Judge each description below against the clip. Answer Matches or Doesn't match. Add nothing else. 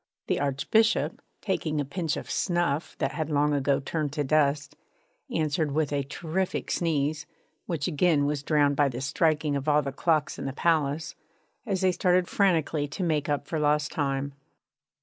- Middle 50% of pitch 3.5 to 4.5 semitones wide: Doesn't match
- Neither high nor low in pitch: Matches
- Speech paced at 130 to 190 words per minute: Matches